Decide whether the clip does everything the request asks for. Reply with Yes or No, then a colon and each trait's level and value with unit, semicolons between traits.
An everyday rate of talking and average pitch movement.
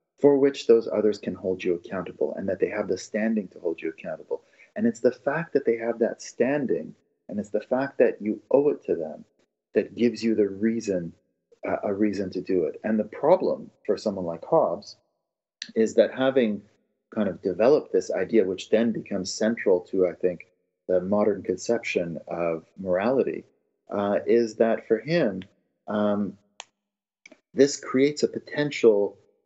No: average, 175 wpm; wide, 6.0 semitones